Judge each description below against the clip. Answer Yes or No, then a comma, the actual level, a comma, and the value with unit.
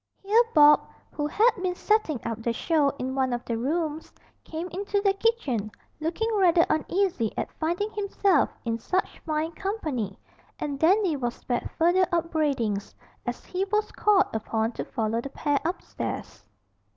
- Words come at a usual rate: Yes, average, 155 wpm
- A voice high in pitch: Yes, very high, 315 Hz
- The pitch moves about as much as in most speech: No, wide, 7.2 semitones